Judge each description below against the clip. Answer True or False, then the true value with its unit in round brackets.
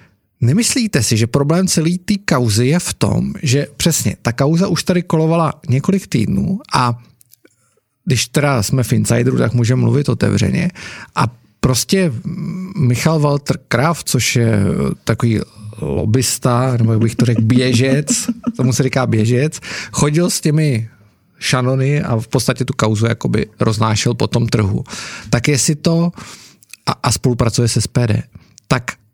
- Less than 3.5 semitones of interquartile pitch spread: False (5.7 semitones)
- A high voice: False (130 Hz)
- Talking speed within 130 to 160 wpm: True (150 wpm)